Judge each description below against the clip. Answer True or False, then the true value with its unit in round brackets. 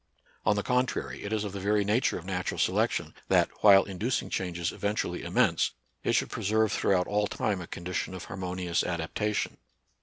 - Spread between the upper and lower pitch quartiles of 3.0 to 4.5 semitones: False (2.6 semitones)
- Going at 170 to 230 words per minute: True (180 wpm)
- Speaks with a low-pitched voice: True (100 Hz)